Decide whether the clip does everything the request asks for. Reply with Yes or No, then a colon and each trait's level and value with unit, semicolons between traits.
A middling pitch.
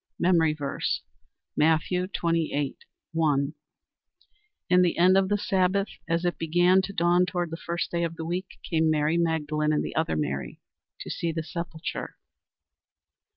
Yes: medium, 170 Hz